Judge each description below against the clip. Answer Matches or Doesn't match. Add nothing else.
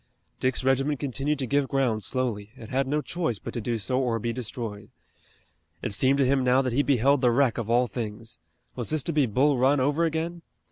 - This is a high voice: Doesn't match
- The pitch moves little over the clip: Doesn't match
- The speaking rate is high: Matches